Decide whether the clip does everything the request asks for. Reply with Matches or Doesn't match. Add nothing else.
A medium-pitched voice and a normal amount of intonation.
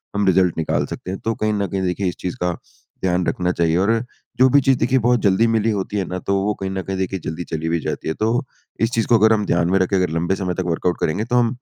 Doesn't match